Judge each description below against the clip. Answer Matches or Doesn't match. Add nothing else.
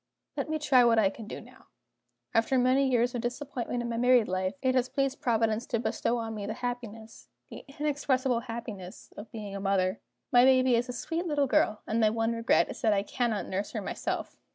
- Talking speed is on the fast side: Matches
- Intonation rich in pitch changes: Doesn't match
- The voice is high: Matches